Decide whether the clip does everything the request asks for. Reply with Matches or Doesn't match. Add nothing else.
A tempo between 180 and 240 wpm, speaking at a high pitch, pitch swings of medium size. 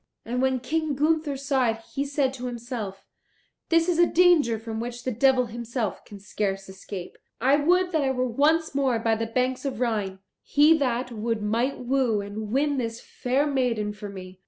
Matches